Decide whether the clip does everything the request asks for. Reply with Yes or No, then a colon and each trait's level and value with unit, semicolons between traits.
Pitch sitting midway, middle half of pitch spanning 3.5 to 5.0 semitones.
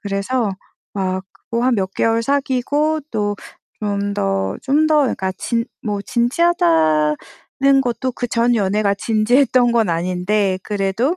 No: high, 215 Hz; average, 4.5 semitones